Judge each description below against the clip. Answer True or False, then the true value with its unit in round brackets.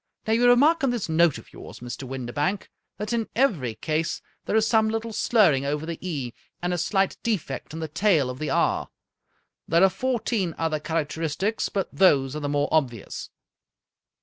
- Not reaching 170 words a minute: False (190 wpm)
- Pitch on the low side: False (170 Hz)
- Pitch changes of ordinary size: False (6.9 semitones)